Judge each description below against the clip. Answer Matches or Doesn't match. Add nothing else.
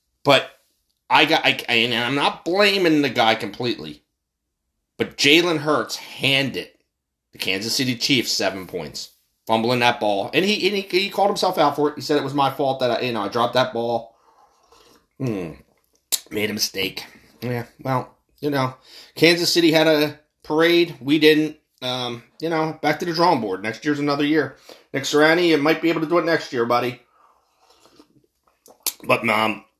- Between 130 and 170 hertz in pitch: Matches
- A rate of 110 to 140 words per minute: Doesn't match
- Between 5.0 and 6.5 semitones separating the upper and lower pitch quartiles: Matches